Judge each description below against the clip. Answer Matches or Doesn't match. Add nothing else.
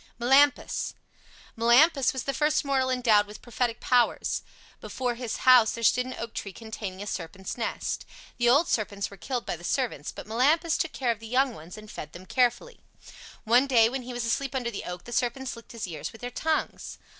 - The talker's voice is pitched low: Doesn't match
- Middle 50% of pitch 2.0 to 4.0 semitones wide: Matches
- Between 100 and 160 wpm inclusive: Doesn't match